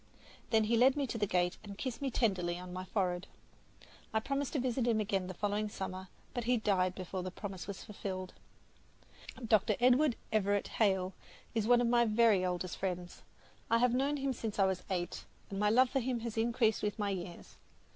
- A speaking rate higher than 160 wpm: Yes, average, 200 wpm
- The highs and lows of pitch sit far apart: No, average, 4.1 semitones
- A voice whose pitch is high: Yes, high, 210 Hz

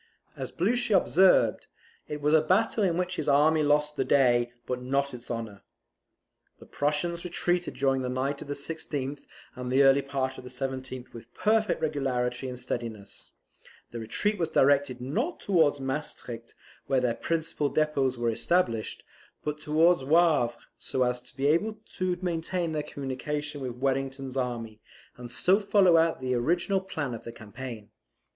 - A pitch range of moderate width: Yes, average, 4.6 semitones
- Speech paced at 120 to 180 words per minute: Yes, average, 165 wpm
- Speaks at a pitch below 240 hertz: Yes, medium, 140 Hz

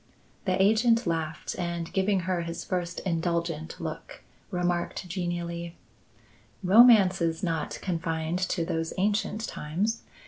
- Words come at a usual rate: No, slow, 115 wpm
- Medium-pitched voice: Yes, medium, 175 Hz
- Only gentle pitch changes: Yes, narrow, 2.2 semitones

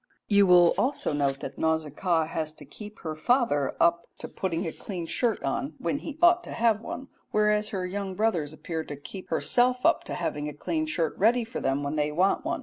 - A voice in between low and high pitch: Yes, medium, 180 Hz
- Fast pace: Yes, fast, 215 wpm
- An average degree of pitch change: No, wide, 6.5 semitones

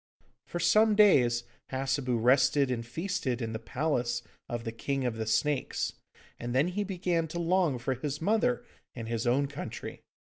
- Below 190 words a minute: Yes, average, 170 wpm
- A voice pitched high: No, low, 135 Hz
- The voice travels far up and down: Yes, wide, 6.2 semitones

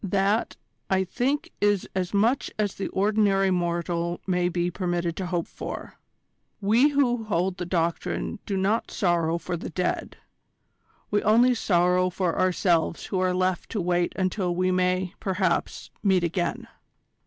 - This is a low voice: No, medium, 185 Hz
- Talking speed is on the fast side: No, average, 150 wpm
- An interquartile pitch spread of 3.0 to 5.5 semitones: No, narrow, 2.5 semitones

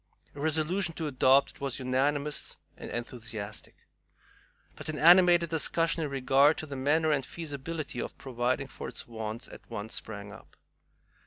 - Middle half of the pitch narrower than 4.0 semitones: No, average, 4.4 semitones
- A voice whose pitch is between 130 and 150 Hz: Yes, medium, 140 Hz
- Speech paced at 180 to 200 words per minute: No, average, 155 wpm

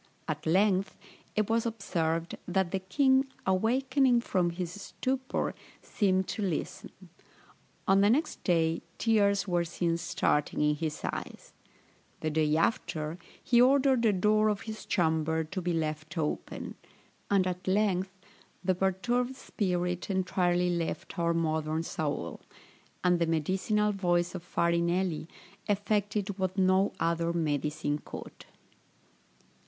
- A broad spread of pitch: No, average, 3.7 semitones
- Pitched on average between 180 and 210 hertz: Yes, medium, 185 Hz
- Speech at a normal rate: No, slow, 125 wpm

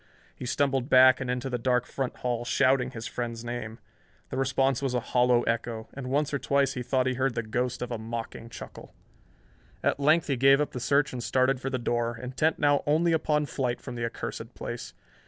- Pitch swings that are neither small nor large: No, narrow, 2.3 semitones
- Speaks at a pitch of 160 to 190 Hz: No, low, 125 Hz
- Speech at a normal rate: No, fast, 210 wpm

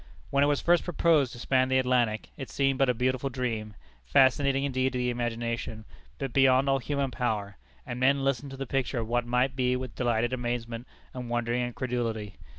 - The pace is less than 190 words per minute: No, average, 195 wpm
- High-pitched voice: No, low, 125 Hz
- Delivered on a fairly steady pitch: Yes, narrow, 2.1 semitones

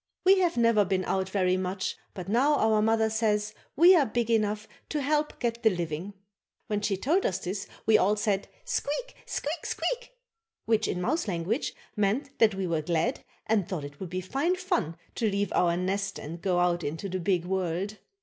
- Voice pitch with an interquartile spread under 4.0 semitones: No, average, 4.3 semitones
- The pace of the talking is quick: No, average, 195 wpm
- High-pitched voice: Yes, high, 205 Hz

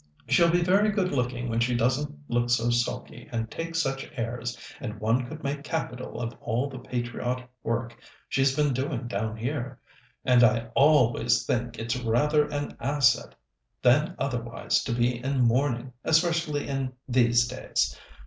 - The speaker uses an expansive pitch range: No, average, 3.3 semitones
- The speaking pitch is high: No, low, 125 Hz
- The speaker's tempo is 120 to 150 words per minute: No, average, 160 wpm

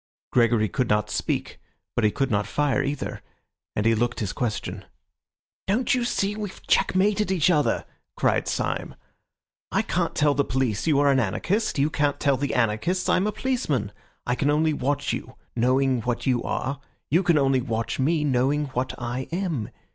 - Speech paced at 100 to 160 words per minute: No, average, 180 wpm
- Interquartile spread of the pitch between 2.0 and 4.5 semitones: No, average, 5.0 semitones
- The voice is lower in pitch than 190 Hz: Yes, medium, 140 Hz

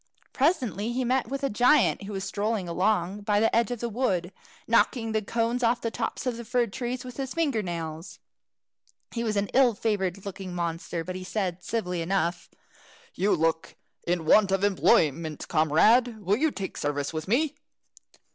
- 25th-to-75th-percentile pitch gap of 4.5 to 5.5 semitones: Yes, average, 5.0 semitones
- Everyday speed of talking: Yes, average, 180 wpm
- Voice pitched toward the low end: No, high, 205 Hz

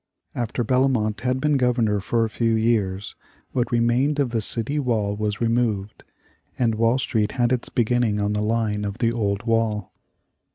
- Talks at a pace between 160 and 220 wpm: Yes, average, 170 wpm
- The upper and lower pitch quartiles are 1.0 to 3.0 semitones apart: Yes, narrow, 2.6 semitones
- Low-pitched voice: Yes, low, 115 Hz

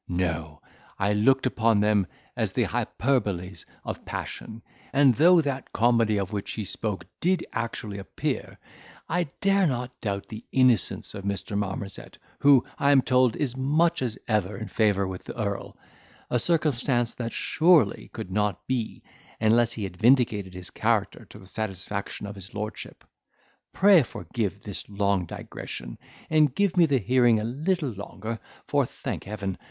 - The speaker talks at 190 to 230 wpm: No, average, 160 wpm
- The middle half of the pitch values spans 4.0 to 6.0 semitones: Yes, average, 4.7 semitones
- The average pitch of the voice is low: Yes, low, 110 Hz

